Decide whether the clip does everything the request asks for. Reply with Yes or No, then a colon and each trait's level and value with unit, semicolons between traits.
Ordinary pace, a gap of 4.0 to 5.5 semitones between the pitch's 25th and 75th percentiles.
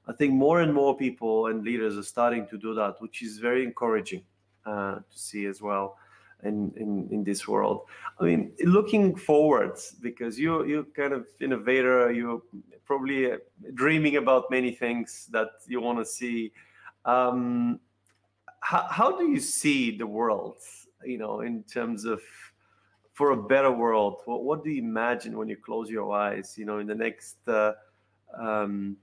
Yes: average, 170 wpm; average, 4.6 semitones